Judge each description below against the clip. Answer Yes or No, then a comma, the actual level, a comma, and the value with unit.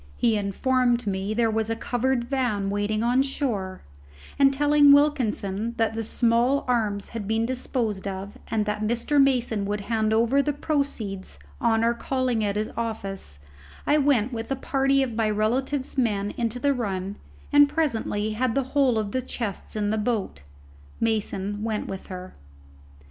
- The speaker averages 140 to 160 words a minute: No, average, 170 wpm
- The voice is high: Yes, high, 230 Hz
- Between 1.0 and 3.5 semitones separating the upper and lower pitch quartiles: No, average, 3.9 semitones